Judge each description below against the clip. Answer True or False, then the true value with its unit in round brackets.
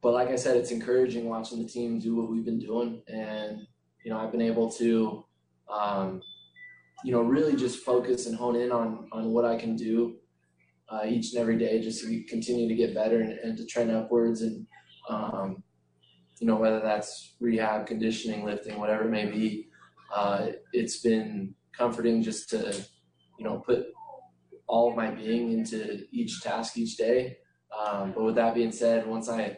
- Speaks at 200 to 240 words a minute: False (185 wpm)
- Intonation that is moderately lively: False (1.7 semitones)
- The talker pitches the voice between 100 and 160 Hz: True (115 Hz)